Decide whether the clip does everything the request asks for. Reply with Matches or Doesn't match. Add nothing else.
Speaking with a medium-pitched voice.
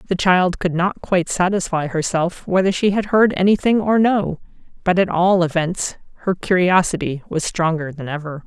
Matches